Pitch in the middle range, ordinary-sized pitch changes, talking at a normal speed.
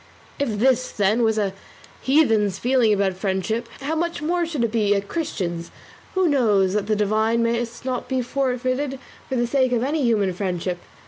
No: high, 235 Hz; average, 4.4 semitones; average, 180 wpm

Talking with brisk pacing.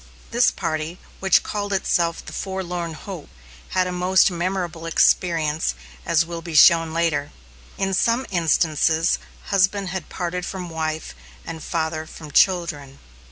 No: slow, 135 wpm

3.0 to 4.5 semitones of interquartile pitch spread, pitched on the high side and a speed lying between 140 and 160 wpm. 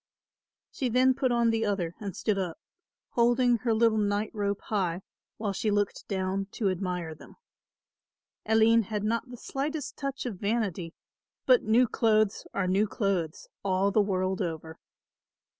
Yes: average, 3.5 semitones; high, 210 Hz; average, 150 wpm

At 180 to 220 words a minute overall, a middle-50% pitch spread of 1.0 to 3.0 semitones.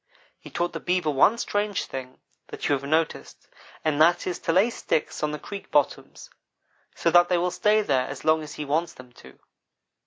No: fast, 205 wpm; average, 3.7 semitones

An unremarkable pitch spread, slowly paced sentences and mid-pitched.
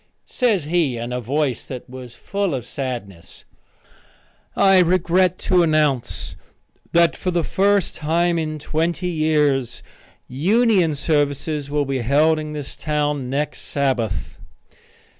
Yes: average, 4.3 semitones; slow, 125 wpm; medium, 150 Hz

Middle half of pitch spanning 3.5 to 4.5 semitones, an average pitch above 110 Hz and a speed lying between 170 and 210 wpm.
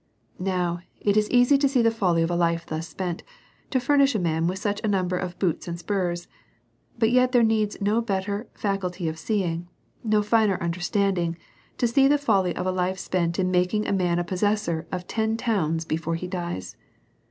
Yes: average, 3.9 semitones; high, 190 Hz; fast, 205 wpm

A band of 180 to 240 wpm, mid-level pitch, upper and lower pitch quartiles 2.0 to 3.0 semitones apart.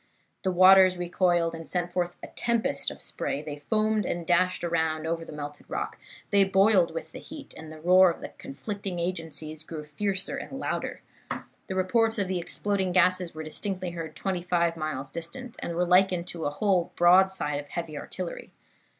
Yes: average, 185 wpm; medium, 175 Hz; average, 2.7 semitones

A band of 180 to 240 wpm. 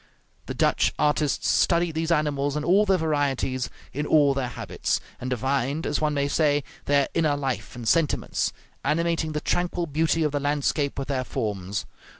No: average, 170 wpm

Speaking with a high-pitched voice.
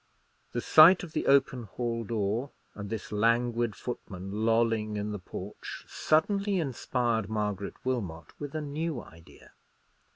No: low, 115 Hz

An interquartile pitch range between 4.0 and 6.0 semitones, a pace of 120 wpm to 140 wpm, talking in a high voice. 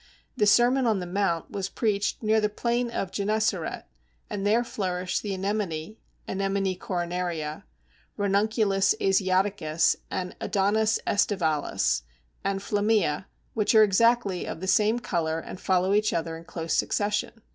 No: average, 2.9 semitones; slow, 135 wpm; high, 195 Hz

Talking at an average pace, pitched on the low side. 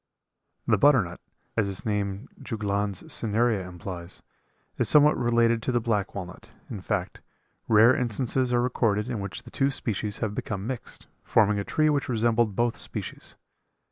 Yes: average, 155 wpm; low, 110 Hz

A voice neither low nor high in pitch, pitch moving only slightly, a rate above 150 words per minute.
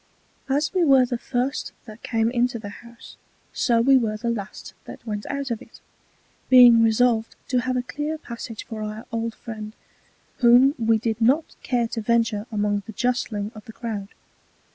No: high, 235 Hz; narrow, 2.2 semitones; average, 180 wpm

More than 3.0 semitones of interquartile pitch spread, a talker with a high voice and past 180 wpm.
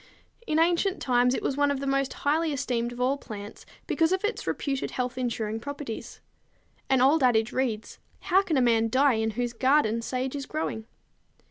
Yes: average, 3.6 semitones; very high, 260 Hz; average, 190 wpm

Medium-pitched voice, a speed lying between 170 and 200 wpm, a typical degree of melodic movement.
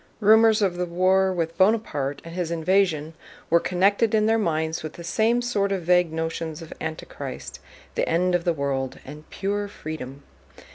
Yes: medium, 175 Hz; average, 175 wpm; average, 3.9 semitones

